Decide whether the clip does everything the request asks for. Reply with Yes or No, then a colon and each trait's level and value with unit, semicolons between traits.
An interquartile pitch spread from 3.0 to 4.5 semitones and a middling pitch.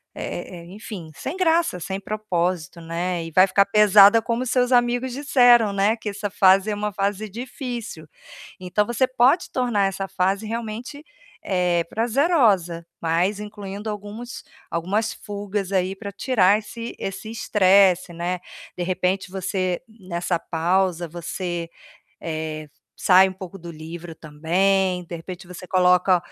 No: average, 3.5 semitones; high, 195 Hz